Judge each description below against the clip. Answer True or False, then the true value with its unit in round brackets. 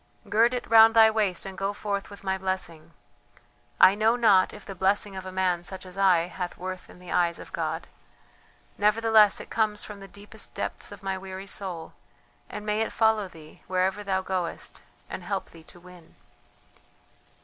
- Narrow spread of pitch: True (2.2 semitones)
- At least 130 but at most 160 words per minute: False (185 wpm)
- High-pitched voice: True (195 Hz)